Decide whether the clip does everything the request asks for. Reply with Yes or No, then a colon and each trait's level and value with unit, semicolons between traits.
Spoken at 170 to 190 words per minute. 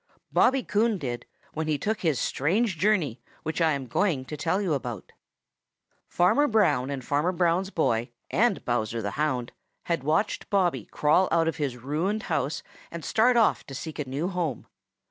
Yes: average, 175 wpm